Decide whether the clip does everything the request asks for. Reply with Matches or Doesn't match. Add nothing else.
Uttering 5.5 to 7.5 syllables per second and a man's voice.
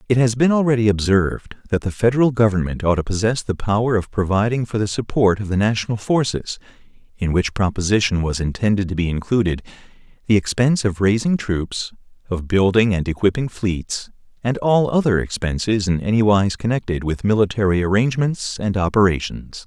Matches